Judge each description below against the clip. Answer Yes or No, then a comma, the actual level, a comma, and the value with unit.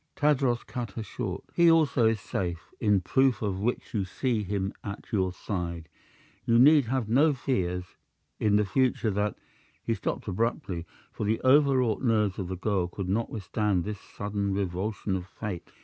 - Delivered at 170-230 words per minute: Yes, average, 175 wpm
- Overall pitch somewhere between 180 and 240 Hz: No, low, 105 Hz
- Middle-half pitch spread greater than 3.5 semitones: Yes, average, 4.3 semitones